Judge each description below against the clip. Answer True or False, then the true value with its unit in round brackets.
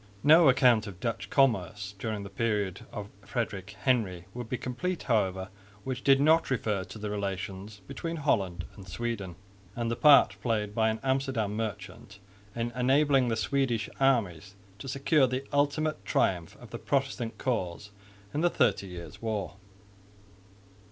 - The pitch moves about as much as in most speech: True (5.0 semitones)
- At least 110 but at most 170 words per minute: True (150 wpm)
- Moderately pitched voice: False (115 Hz)